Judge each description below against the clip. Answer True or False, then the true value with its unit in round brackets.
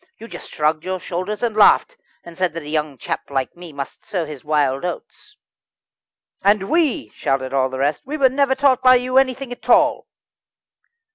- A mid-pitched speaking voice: True (180 Hz)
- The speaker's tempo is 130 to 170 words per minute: False (185 wpm)